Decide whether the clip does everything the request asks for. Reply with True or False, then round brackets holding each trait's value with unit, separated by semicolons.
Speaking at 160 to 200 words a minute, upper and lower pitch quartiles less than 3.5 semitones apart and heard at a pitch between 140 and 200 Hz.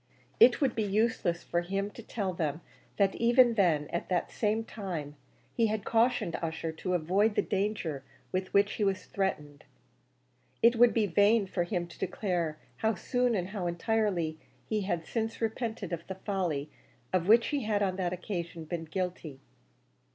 False (175 wpm; 4.2 semitones; 190 Hz)